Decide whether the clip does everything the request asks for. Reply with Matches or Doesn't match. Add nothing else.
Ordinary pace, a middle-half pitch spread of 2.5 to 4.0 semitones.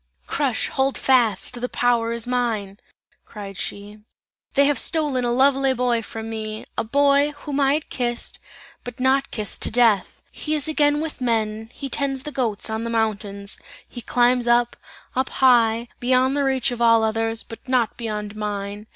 Matches